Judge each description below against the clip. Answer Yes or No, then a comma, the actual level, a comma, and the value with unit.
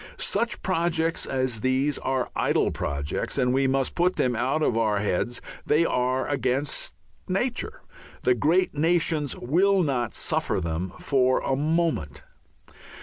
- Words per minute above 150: No, average, 140 wpm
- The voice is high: No, low, 135 Hz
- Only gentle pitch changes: No, average, 4.7 semitones